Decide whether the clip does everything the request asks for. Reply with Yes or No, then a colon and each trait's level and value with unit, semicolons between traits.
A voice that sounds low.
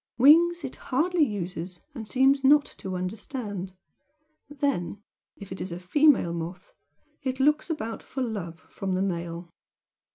No: high, 220 Hz